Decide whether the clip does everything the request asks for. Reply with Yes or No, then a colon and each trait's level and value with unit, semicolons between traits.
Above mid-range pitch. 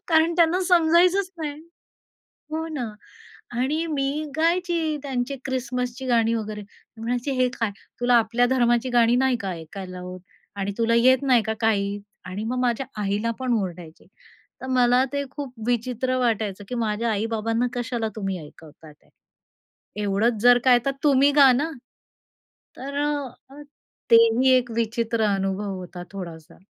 Yes: high, 240 Hz